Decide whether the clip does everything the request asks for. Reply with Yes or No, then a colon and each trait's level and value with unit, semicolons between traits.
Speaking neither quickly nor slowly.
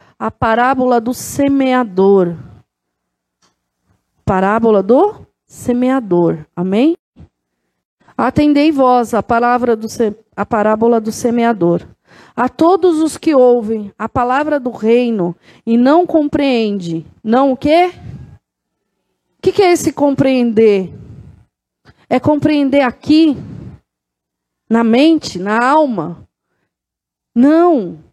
No: slow, 100 wpm